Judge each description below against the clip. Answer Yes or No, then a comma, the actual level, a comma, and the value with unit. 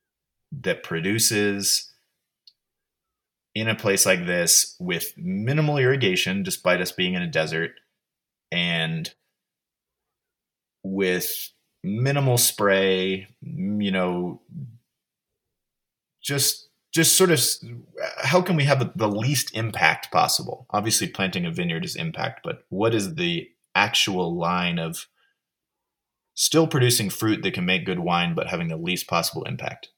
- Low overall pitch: Yes, low, 110 Hz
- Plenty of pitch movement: Yes, wide, 9.0 semitones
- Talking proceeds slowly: Yes, slow, 120 wpm